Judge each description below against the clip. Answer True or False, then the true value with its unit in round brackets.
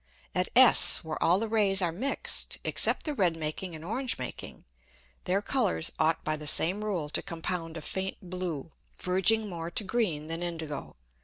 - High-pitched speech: False (180 Hz)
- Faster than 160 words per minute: True (175 wpm)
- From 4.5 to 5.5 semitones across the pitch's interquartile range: False (4.0 semitones)